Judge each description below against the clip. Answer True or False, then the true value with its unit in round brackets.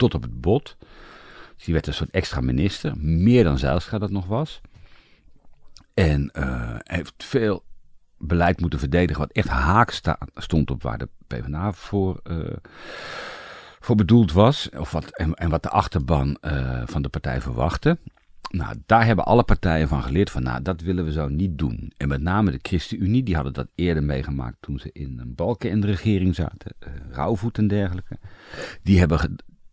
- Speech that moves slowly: False (180 wpm)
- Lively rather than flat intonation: True (6.1 semitones)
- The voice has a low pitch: True (85 Hz)